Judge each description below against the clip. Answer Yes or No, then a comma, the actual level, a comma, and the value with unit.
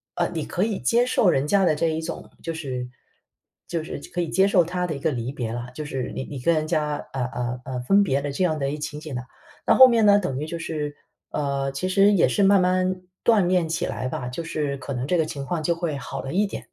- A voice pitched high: No, medium, 155 Hz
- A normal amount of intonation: Yes, average, 4.9 semitones